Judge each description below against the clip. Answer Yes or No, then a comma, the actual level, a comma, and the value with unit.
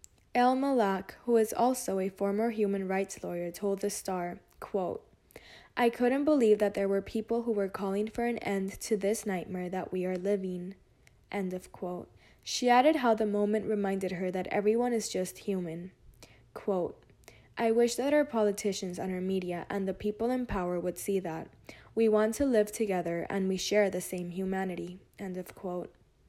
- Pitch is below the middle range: No, high, 200 Hz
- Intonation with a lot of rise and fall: No, average, 3.3 semitones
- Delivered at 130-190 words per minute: Yes, average, 185 wpm